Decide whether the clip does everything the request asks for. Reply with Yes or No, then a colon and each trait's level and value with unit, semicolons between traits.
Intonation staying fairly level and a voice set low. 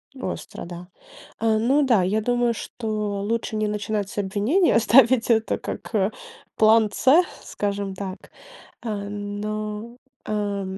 No: narrow, 2.2 semitones; high, 215 Hz